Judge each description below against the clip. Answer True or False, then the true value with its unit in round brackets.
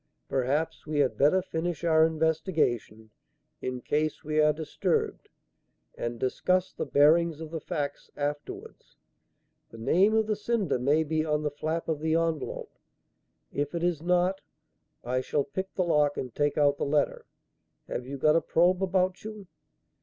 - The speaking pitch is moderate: True (155 Hz)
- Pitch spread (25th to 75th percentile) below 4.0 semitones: True (3.2 semitones)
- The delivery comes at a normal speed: True (160 wpm)